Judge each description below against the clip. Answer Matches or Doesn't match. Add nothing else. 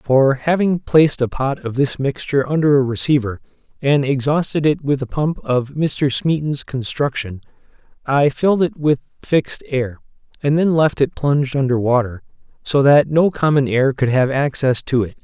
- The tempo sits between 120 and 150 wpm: Doesn't match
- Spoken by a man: Matches